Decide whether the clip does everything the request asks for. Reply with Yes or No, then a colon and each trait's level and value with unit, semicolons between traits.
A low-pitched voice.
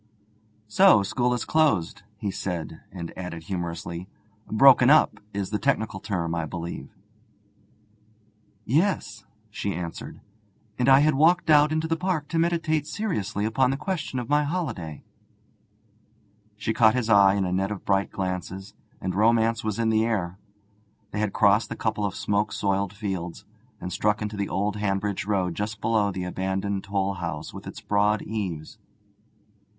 Yes: low, 105 Hz